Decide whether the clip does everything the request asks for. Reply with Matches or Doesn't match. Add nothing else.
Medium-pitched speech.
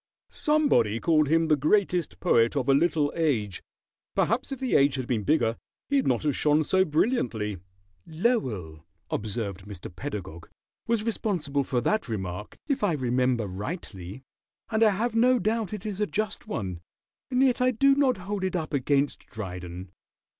Matches